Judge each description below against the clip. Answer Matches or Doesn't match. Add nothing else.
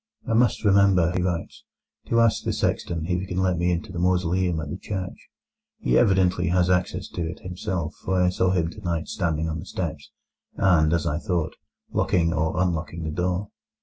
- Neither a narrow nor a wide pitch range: Doesn't match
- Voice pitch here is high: Doesn't match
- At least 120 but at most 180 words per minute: Doesn't match